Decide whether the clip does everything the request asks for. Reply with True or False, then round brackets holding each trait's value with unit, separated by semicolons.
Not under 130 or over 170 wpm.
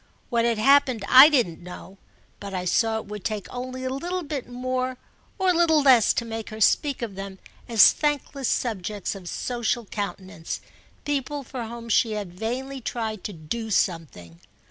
True (165 wpm)